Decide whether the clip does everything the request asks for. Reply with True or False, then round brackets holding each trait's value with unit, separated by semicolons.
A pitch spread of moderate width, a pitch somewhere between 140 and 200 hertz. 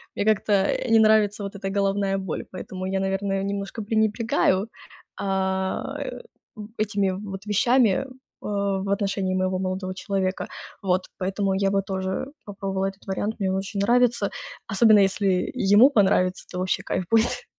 False (1.4 semitones; 195 Hz)